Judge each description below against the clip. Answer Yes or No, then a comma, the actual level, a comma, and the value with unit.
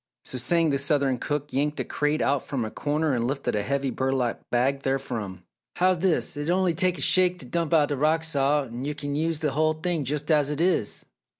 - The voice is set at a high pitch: No, medium, 145 Hz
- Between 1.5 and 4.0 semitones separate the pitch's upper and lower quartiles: Yes, average, 3.1 semitones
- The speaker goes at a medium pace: No, fast, 225 wpm